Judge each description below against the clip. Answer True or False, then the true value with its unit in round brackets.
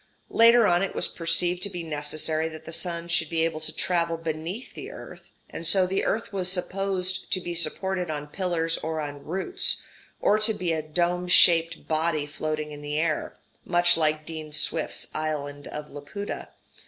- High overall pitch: False (165 Hz)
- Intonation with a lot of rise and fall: False (2.6 semitones)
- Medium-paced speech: True (180 wpm)